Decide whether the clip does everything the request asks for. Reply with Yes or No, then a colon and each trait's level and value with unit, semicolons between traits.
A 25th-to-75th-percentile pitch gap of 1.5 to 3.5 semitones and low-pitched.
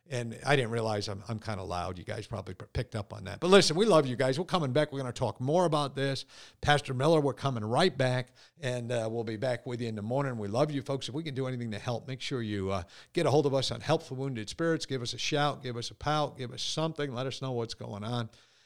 No: average, 3.9 semitones; low, 125 Hz